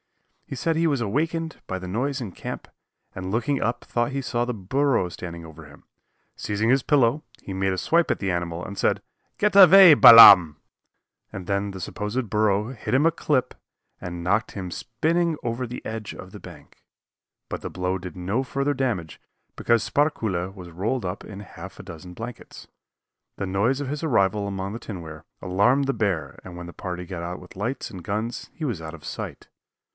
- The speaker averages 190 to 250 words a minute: Yes, average, 195 wpm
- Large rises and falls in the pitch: Yes, wide, 6.2 semitones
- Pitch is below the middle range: Yes, low, 105 Hz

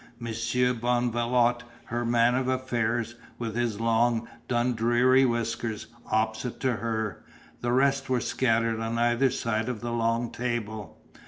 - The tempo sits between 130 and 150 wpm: Yes, slow, 135 wpm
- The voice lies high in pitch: No, low, 120 Hz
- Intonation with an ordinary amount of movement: No, narrow, 1.3 semitones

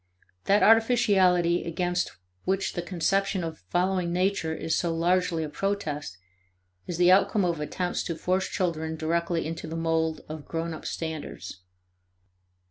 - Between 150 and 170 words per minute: No, average, 140 wpm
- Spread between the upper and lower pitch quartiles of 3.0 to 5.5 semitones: No, narrow, 2.4 semitones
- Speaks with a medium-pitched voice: Yes, medium, 170 Hz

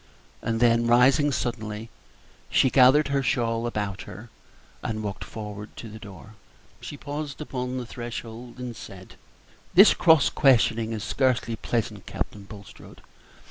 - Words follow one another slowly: Yes, slow, 130 wpm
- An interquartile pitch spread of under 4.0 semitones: Yes, average, 3.0 semitones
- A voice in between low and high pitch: No, low, 115 Hz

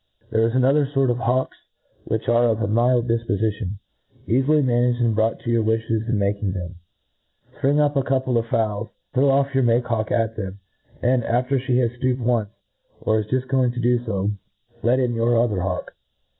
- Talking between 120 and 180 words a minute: No, average, 200 wpm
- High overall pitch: No, low, 120 Hz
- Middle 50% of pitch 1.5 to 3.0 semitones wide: Yes, narrow, 2.5 semitones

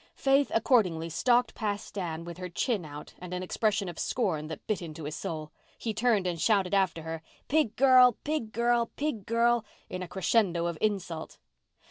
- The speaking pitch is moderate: No, high, 200 Hz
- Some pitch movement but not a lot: No, wide, 5.7 semitones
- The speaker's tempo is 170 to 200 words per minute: Yes, average, 180 wpm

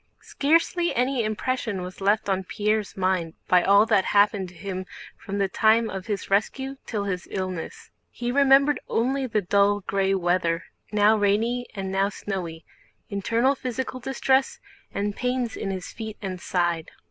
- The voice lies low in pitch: No, high, 205 Hz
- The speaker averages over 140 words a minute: Yes, average, 160 wpm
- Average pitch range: Yes, average, 4.1 semitones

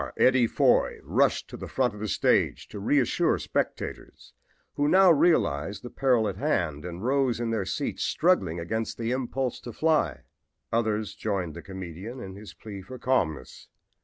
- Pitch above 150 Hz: No, low, 110 Hz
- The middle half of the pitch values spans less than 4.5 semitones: No, average, 5.3 semitones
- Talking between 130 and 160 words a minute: No, average, 170 wpm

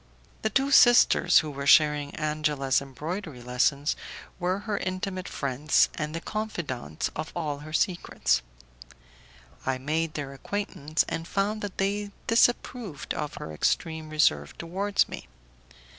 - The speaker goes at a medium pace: No, slow, 130 wpm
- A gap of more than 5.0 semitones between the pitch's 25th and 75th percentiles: Yes, wide, 5.5 semitones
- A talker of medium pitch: Yes, medium, 155 Hz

